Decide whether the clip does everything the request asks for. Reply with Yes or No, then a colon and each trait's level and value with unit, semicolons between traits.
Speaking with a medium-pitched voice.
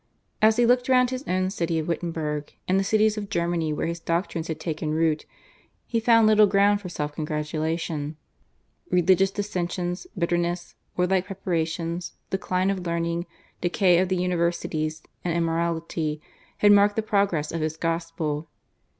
Yes: medium, 175 Hz